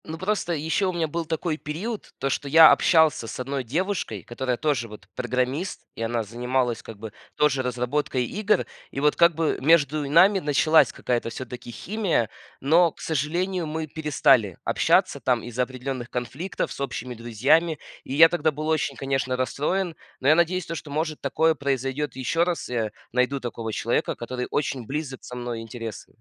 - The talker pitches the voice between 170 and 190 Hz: No, medium, 140 Hz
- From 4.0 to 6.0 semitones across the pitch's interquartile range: Yes, average, 4.5 semitones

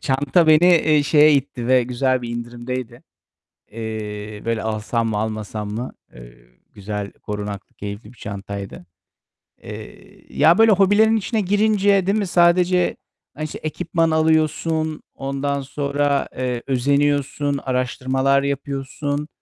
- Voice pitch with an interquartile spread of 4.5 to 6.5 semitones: Yes, wide, 5.5 semitones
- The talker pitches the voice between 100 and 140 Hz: Yes, low, 135 Hz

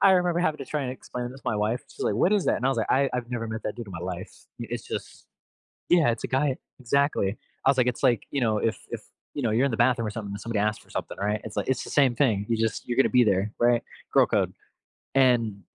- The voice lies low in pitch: Yes, low, 120 Hz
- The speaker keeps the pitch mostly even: No, average, 3.6 semitones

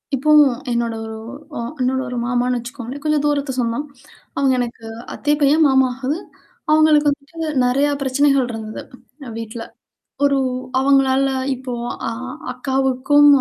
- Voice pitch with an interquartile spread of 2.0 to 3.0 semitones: Yes, narrow, 2.6 semitones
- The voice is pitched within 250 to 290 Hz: Yes, very high, 265 Hz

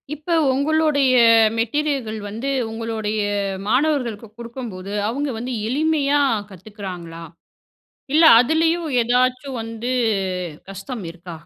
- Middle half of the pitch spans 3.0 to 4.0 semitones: No, average, 4.8 semitones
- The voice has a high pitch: Yes, high, 245 Hz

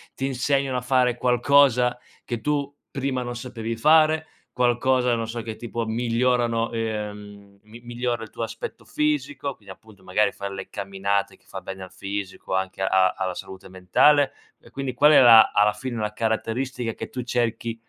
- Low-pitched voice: Yes, low, 115 Hz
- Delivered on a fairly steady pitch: No, average, 3.4 semitones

